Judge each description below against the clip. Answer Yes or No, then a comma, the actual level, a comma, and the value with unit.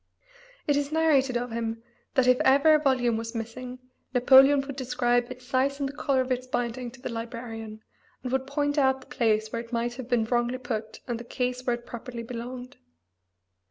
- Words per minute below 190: No, average, 200 wpm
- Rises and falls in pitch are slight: Yes, narrow, 2.1 semitones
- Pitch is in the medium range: No, very high, 250 Hz